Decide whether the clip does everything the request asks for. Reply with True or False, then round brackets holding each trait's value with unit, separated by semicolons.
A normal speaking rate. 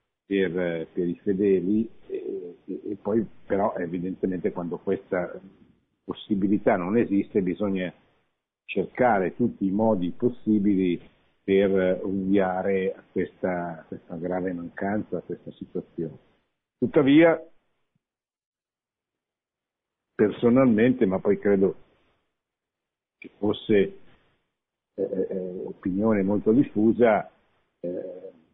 False (90 wpm)